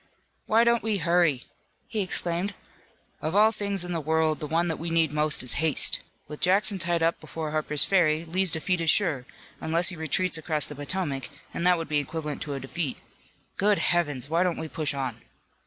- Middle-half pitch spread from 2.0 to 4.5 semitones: Yes, average, 3.2 semitones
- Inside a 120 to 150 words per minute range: No, average, 200 wpm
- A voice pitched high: No, medium, 165 Hz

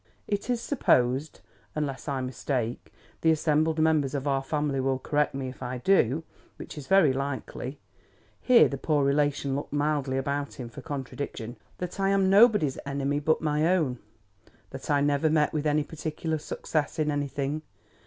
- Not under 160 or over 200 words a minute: Yes, average, 165 wpm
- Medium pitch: Yes, medium, 145 Hz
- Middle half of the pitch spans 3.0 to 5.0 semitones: No, narrow, 2.6 semitones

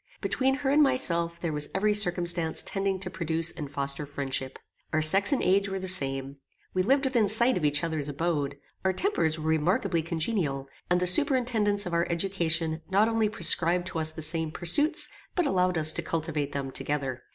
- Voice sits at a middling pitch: Yes, medium, 170 Hz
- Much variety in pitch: No, average, 4.7 semitones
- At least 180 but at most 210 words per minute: Yes, average, 190 wpm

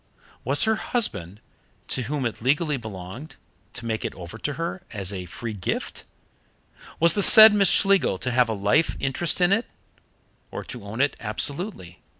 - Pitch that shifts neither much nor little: No, wide, 8.2 semitones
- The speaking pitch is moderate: No, low, 130 Hz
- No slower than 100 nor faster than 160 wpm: No, average, 170 wpm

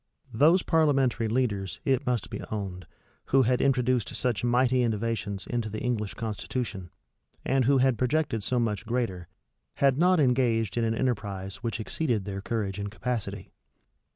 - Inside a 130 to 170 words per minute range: Yes, average, 155 wpm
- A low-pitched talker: Yes, low, 115 Hz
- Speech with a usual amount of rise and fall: Yes, average, 3.5 semitones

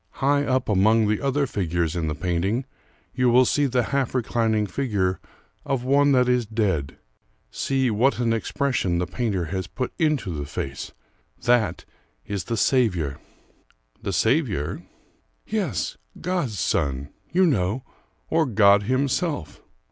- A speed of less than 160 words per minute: Yes, average, 140 wpm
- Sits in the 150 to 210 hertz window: No, low, 115 Hz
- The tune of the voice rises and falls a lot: Yes, wide, 6.1 semitones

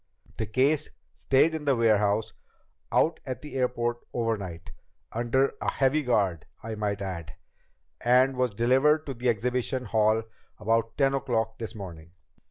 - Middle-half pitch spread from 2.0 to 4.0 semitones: Yes, average, 3.7 semitones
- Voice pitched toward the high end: No, low, 120 Hz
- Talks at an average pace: Yes, average, 145 wpm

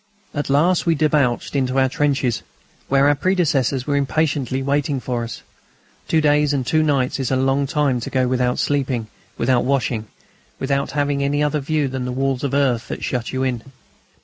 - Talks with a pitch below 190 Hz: Yes, low, 135 Hz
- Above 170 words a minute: Yes, average, 185 wpm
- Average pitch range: No, narrow, 2.3 semitones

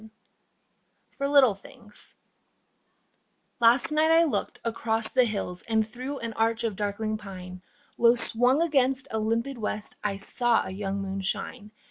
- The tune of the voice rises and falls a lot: No, average, 3.6 semitones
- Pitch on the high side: Yes, high, 225 Hz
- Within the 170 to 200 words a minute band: No, average, 150 wpm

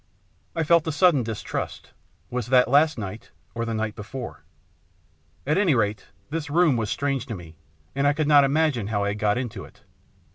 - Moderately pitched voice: No, low, 125 Hz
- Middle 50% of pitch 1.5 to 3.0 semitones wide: No, wide, 5.5 semitones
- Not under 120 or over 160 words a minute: No, average, 185 wpm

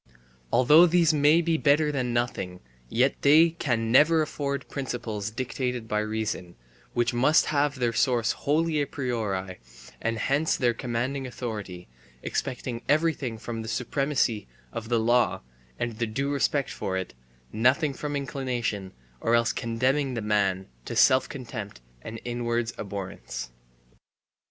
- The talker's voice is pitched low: Yes, low, 120 Hz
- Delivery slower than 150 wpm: Yes, average, 140 wpm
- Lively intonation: No, average, 4.0 semitones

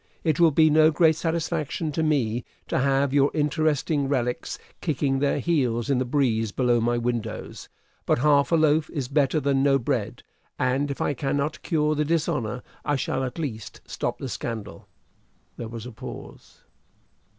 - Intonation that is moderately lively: Yes, average, 3.8 semitones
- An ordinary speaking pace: Yes, average, 170 wpm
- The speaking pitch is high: No, medium, 140 Hz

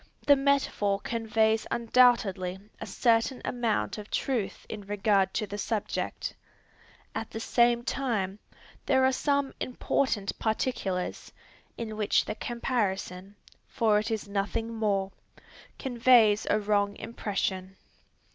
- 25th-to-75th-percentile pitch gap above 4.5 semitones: No, average, 2.9 semitones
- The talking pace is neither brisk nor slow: No, slow, 120 wpm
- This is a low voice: No, high, 220 Hz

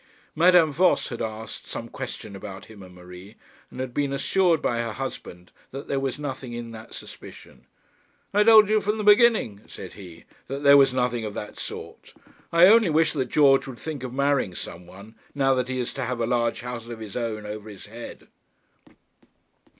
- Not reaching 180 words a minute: No, average, 195 wpm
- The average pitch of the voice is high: No, low, 125 Hz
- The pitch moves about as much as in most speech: Yes, average, 4.9 semitones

